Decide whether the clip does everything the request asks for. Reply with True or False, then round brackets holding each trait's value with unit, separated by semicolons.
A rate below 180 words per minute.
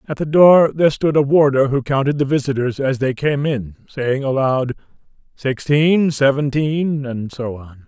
True (170 wpm)